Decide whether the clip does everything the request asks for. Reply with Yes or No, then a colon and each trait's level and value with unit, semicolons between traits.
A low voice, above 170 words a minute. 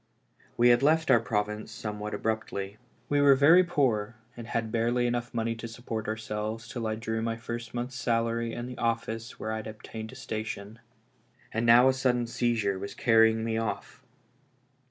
Yes: low, 115 Hz; average, 185 wpm